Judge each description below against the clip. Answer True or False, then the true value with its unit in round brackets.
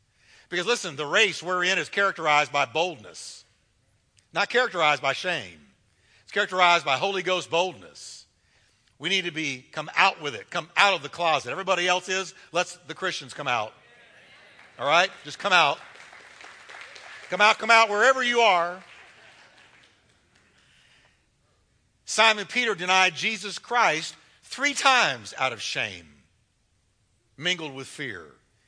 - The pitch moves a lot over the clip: True (6.5 semitones)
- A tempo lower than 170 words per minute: True (140 wpm)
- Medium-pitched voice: True (175 Hz)